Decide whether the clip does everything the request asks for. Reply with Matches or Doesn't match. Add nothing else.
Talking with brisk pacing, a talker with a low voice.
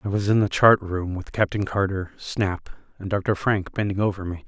Matches